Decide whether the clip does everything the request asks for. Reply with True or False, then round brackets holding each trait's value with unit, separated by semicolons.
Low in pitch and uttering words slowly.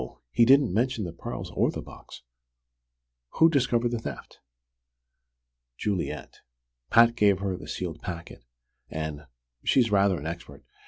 True (100 Hz; 130 wpm)